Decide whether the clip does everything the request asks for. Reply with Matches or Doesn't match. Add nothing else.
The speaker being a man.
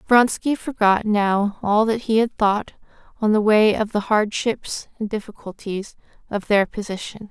Doesn't match